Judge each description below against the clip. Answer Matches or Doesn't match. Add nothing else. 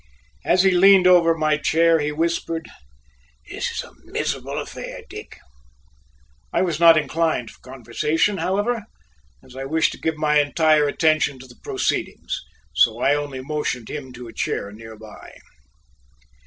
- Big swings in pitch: Doesn't match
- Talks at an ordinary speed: Matches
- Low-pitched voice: Doesn't match